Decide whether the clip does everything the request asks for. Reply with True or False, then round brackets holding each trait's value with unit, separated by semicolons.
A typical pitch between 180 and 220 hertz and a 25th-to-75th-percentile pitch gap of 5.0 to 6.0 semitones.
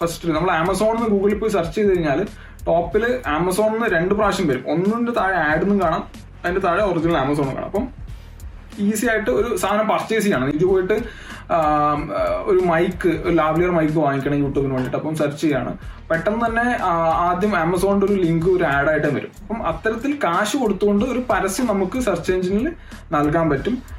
True (185 Hz; 5.3 semitones)